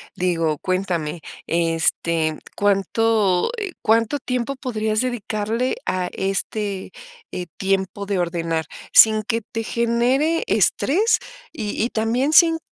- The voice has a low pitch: No, high, 215 Hz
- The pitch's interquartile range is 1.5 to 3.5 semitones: No, average, 4.7 semitones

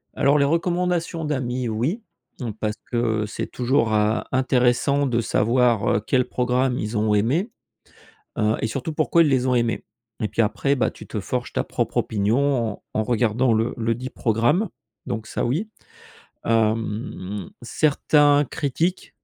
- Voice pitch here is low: Yes, low, 125 Hz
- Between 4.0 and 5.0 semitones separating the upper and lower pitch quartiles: Yes, average, 4.3 semitones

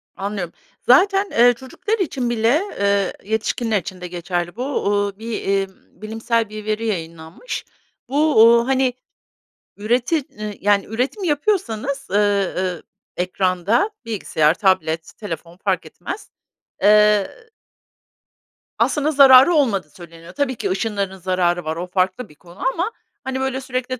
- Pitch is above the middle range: Yes, high, 215 Hz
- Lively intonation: Yes, wide, 5.9 semitones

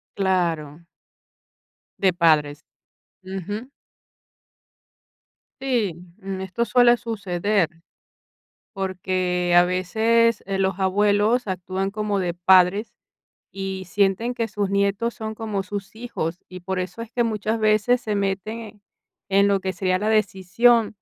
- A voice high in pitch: Yes, high, 195 Hz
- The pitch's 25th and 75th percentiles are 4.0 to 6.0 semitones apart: No, average, 2.8 semitones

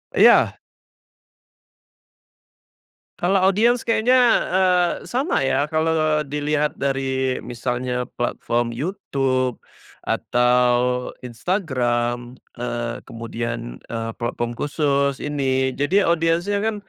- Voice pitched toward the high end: No, low, 135 Hz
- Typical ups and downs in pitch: No, wide, 6.0 semitones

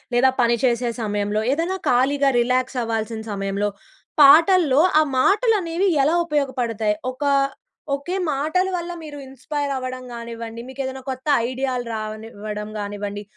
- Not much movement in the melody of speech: No, average, 4.3 semitones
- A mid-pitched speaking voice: No, very high, 255 Hz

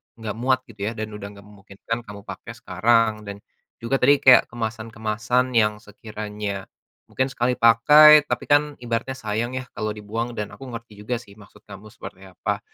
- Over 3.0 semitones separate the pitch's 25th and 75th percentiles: No, average, 2.7 semitones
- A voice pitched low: Yes, low, 110 Hz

